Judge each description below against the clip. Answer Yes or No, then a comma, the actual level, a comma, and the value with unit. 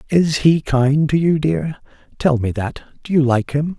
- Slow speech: No, fast, 205 wpm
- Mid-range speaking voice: Yes, medium, 145 Hz